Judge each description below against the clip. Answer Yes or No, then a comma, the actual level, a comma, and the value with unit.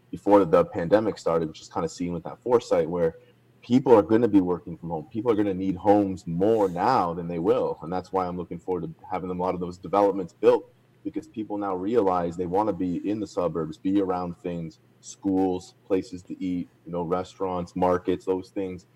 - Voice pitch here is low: Yes, very low, 95 Hz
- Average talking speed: No, fast, 210 wpm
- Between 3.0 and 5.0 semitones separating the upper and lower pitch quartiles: No, narrow, 2.4 semitones